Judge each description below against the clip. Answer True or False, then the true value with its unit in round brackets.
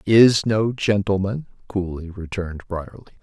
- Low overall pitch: True (100 Hz)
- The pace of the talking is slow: True (110 wpm)